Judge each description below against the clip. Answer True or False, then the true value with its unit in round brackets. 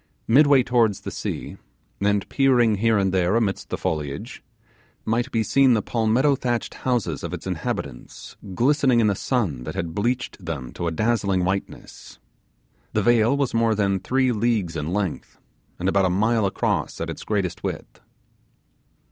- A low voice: True (110 Hz)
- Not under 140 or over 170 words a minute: True (165 wpm)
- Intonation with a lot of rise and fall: False (4.1 semitones)